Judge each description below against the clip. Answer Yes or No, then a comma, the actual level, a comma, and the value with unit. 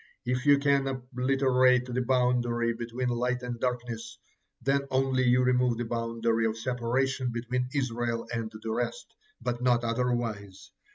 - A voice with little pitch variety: Yes, narrow, 1.6 semitones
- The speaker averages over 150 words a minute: No, average, 145 wpm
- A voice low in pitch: Yes, low, 125 Hz